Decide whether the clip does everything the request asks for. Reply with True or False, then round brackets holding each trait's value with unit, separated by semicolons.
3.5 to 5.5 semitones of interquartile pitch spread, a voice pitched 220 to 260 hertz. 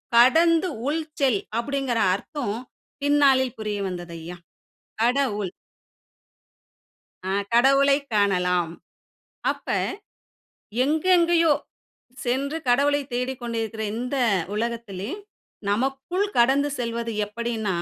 True (4.6 semitones; 245 Hz)